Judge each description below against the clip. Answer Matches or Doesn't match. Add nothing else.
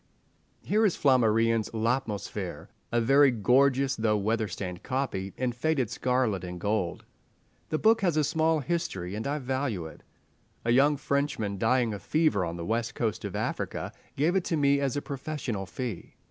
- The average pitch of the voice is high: Doesn't match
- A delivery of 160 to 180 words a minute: Matches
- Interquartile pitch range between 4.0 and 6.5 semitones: Matches